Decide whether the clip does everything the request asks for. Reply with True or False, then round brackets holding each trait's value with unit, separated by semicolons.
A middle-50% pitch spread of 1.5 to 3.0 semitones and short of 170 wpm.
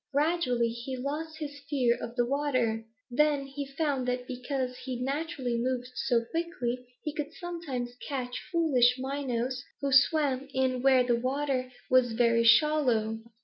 True (2.7 semitones; 145 wpm)